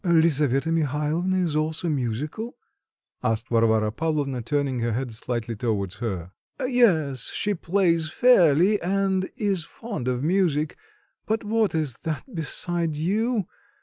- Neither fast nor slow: No, slow, 125 wpm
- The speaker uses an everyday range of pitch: No, wide, 6.7 semitones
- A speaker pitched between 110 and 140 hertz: No, medium, 155 Hz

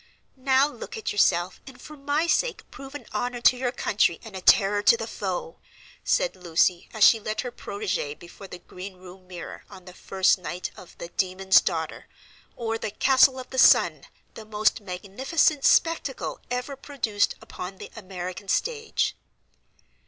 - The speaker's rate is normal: Yes, average, 165 wpm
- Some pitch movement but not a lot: No, wide, 6.1 semitones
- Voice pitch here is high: Yes, high, 210 Hz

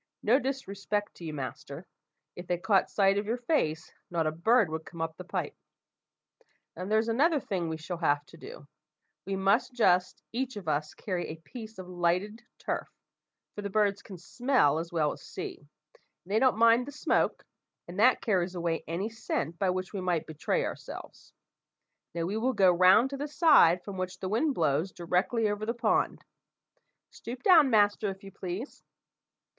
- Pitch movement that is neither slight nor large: Yes, average, 4.9 semitones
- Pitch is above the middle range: Yes, high, 195 Hz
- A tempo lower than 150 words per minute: No, average, 185 wpm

